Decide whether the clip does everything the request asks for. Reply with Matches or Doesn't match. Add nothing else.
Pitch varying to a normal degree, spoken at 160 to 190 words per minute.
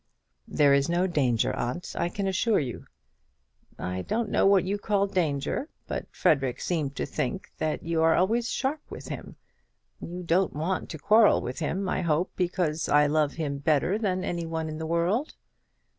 Matches